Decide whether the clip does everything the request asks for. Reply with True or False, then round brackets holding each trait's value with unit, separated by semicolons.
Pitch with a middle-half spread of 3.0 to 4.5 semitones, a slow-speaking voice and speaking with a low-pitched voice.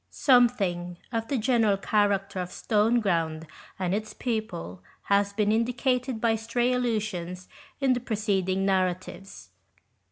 False (3.9 semitones; 120 wpm; 210 Hz)